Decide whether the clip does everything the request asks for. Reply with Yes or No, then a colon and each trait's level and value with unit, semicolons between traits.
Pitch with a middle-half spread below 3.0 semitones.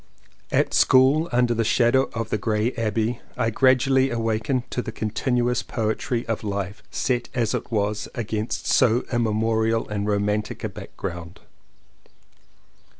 Yes: narrow, 2.4 semitones